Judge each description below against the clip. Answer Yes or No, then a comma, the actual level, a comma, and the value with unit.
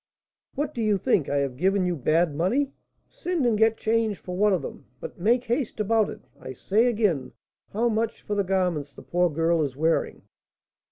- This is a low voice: No, high, 195 Hz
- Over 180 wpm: Yes, average, 200 wpm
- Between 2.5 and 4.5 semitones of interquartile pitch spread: No, wide, 5.4 semitones